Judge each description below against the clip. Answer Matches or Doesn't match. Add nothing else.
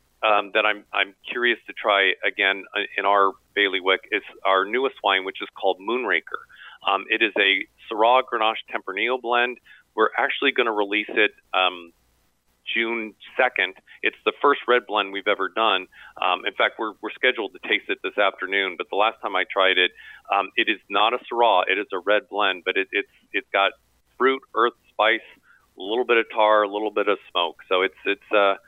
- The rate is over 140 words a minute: Matches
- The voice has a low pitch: Matches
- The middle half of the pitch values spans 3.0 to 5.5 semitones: Matches